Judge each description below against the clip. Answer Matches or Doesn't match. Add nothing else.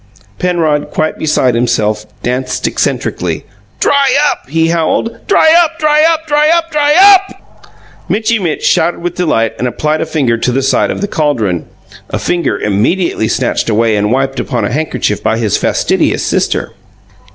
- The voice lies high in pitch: Doesn't match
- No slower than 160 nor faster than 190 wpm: Matches